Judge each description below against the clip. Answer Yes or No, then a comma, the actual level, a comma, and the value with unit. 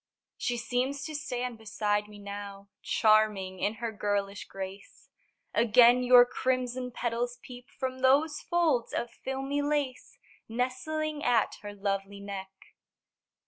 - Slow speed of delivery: Yes, slow, 125 wpm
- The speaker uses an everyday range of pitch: Yes, average, 4.0 semitones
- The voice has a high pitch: Yes, high, 240 Hz